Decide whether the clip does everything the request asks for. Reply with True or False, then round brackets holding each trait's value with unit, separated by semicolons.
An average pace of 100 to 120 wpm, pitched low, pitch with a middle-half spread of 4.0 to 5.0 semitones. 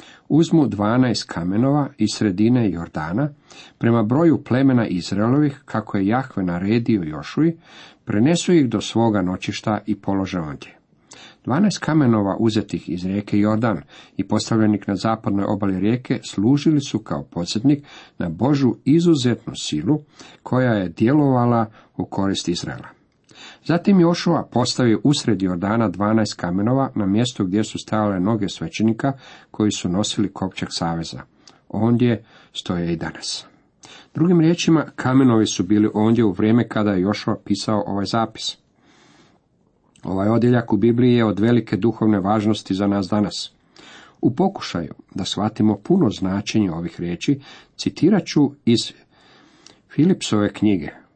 False (130 wpm; 110 Hz; 4.7 semitones)